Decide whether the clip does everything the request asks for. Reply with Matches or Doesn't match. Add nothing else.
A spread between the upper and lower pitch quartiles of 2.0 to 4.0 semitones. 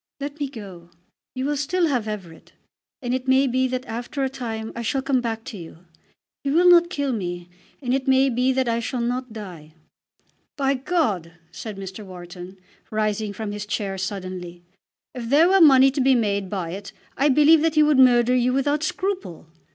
Doesn't match